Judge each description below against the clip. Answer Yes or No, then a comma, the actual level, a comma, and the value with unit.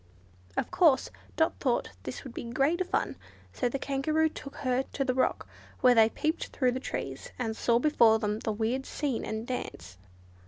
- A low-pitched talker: No, very high, 255 Hz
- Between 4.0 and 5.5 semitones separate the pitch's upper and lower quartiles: No, average, 3.6 semitones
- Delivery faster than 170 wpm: Yes, average, 185 wpm